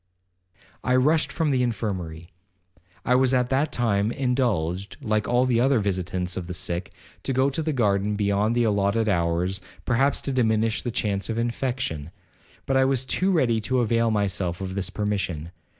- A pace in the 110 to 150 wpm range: No, average, 175 wpm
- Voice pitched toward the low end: Yes, low, 110 Hz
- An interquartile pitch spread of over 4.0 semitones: Yes, average, 4.7 semitones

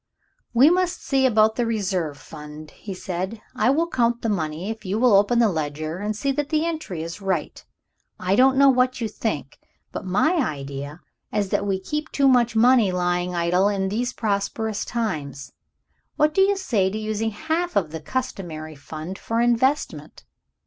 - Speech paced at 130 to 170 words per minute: No, average, 180 wpm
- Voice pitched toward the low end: No, high, 210 Hz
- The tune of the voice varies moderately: No, wide, 6.2 semitones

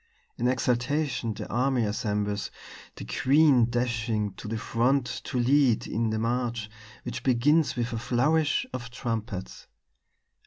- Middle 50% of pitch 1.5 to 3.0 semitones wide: Yes, narrow, 2.5 semitones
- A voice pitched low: Yes, low, 120 Hz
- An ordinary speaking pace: No, slow, 130 wpm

